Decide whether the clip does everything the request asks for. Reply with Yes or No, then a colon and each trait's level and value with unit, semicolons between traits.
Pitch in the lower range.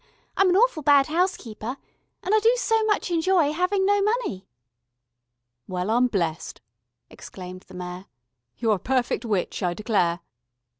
No: very high, 265 Hz